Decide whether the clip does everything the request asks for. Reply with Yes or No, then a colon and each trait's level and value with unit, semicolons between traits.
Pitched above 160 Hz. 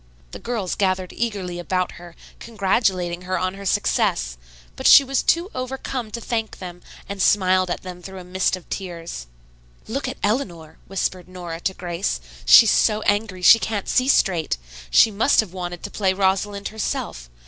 Yes: high, 190 Hz